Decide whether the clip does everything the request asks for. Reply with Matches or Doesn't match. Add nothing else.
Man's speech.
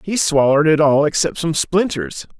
Matches